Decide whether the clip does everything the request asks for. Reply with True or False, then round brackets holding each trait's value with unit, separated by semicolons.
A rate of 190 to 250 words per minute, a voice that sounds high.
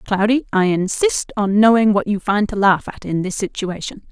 True (205 wpm; 205 Hz)